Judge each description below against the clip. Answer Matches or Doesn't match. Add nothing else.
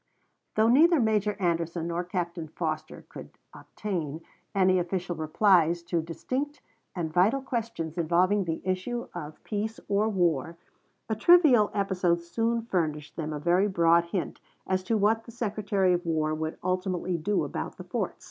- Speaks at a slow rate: Doesn't match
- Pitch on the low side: Doesn't match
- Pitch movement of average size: Matches